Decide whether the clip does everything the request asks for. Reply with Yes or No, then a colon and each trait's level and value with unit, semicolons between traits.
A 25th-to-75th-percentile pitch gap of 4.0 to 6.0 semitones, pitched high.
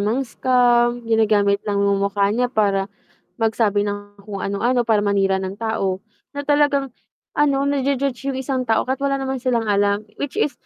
Yes: average, 4.6 semitones; high, 225 Hz